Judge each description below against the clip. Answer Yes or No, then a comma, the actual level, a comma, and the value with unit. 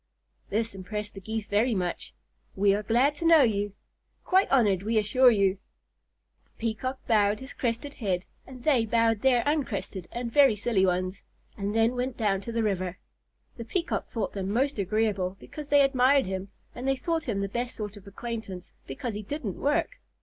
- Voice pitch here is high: Yes, high, 225 Hz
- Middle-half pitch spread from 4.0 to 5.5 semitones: Yes, average, 4.4 semitones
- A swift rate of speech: No, average, 185 wpm